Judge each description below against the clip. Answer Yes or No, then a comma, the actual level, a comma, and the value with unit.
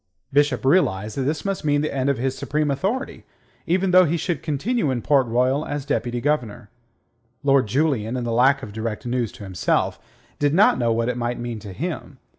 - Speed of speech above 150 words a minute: Yes, fast, 205 wpm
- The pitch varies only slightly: No, average, 3.9 semitones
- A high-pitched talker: No, low, 135 Hz